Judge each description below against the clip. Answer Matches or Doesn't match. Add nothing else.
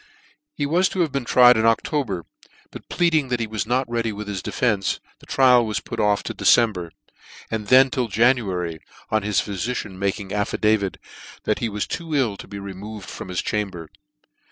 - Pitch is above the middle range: Doesn't match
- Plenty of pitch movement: Doesn't match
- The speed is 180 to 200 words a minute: Matches